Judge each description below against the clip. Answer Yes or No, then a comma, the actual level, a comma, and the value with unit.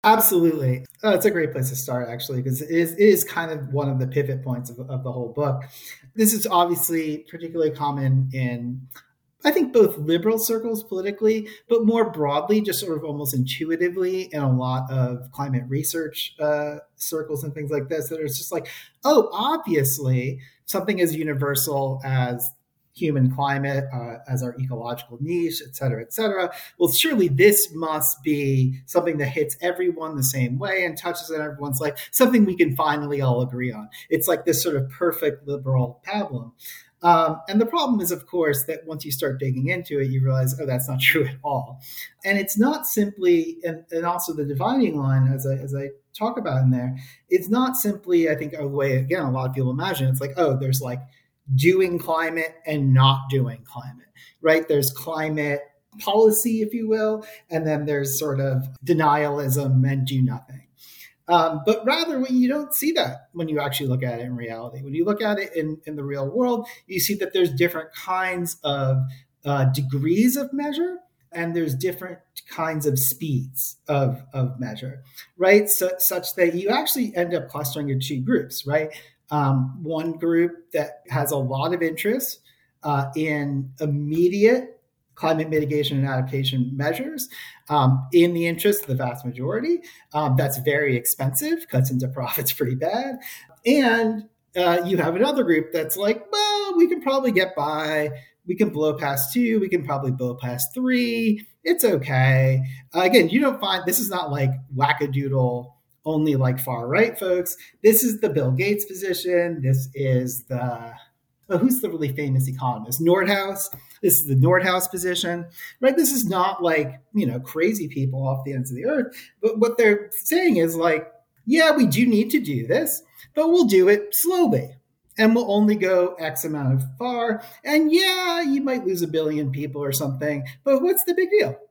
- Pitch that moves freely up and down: Yes, wide, 6.0 semitones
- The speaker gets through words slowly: No, average, 185 wpm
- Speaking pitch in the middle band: Yes, medium, 155 Hz